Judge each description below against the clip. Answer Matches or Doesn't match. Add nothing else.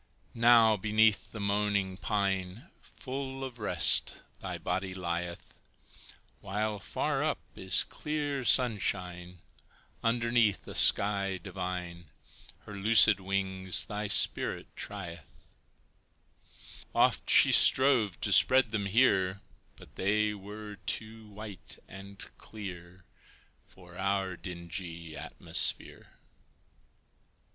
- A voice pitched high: Doesn't match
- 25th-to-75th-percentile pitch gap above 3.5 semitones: Doesn't match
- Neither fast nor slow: Doesn't match